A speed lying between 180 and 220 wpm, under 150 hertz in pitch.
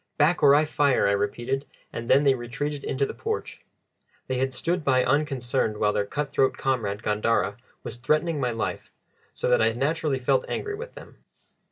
Yes: average, 185 wpm; low, 135 Hz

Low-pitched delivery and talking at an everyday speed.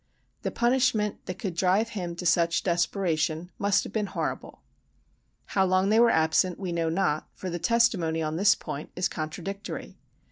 No: medium, 185 Hz; average, 170 wpm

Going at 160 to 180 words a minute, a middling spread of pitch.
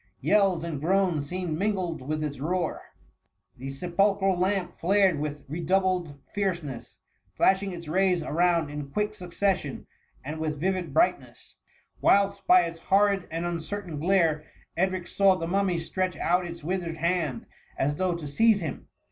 No: average, 150 wpm; average, 3.5 semitones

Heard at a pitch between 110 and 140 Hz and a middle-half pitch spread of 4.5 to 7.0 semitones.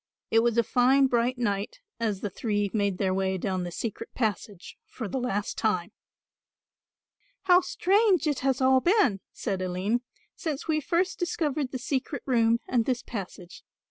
No: high, 235 Hz; average, 5.2 semitones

